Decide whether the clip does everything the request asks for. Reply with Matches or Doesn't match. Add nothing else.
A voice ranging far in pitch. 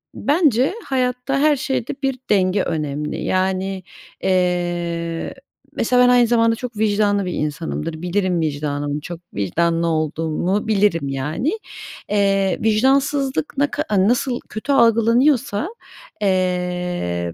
Matches